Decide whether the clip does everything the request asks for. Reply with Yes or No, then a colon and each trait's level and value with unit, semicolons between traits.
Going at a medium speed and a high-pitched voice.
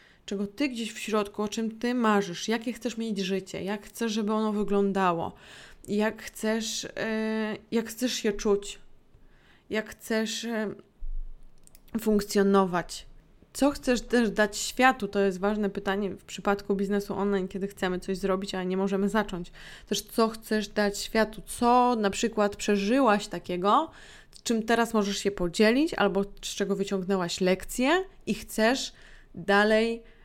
Yes: average, 145 wpm; high, 210 Hz